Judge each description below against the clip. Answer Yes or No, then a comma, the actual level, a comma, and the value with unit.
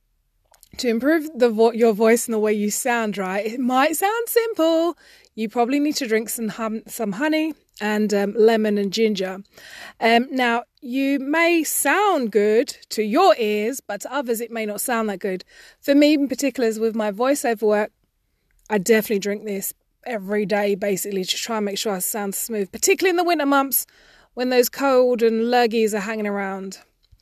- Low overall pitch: No, high, 230 Hz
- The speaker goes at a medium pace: Yes, average, 185 wpm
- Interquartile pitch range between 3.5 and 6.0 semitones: Yes, average, 4.6 semitones